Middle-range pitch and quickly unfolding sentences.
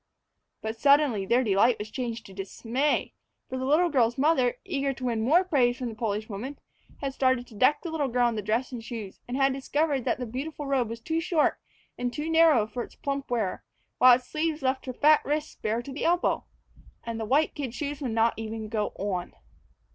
No: very high, 255 Hz; fast, 215 wpm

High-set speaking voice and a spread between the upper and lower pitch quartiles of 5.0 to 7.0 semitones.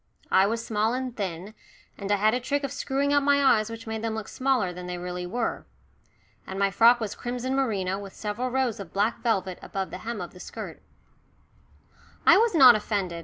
No: high, 220 Hz; average, 4.5 semitones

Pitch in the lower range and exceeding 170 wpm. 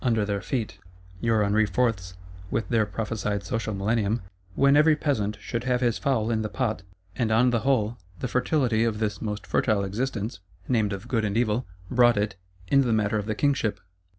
Yes: low, 110 Hz; average, 185 wpm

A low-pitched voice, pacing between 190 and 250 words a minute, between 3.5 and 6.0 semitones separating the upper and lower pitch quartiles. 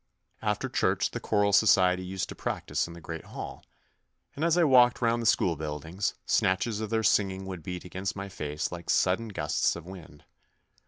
Yes: very low, 95 Hz; average, 195 wpm; average, 4.2 semitones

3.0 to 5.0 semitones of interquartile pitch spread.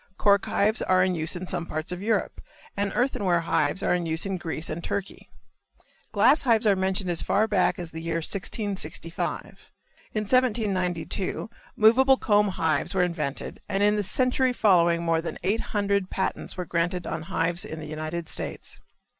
Yes: average, 3.6 semitones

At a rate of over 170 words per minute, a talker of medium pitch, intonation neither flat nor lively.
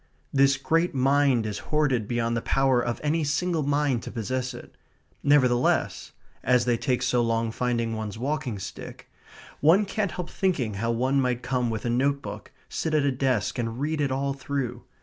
No: average, 180 wpm; low, 130 Hz; average, 3.1 semitones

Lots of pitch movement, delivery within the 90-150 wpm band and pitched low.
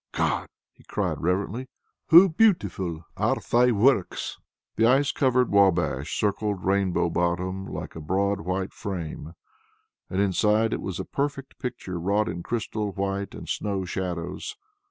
No: average, 4.2 semitones; average, 140 wpm; low, 100 Hz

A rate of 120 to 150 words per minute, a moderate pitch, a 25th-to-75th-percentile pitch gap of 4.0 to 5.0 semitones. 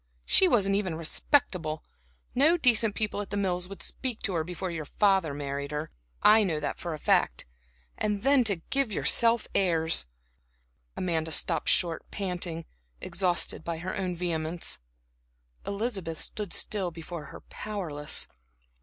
Yes: average, 145 wpm; medium, 180 Hz; average, 4.3 semitones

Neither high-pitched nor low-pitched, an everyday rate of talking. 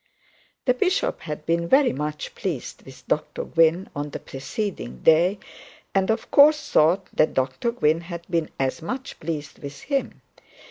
Yes: medium, 165 Hz; average, 155 wpm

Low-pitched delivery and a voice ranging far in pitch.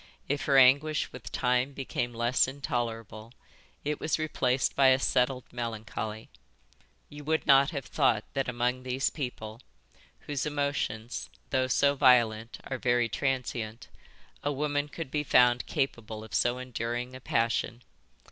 No: low, 125 Hz; average, 2.9 semitones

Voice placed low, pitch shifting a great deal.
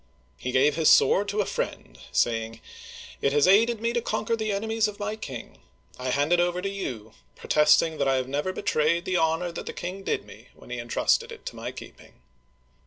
No: medium, 170 Hz; wide, 7.0 semitones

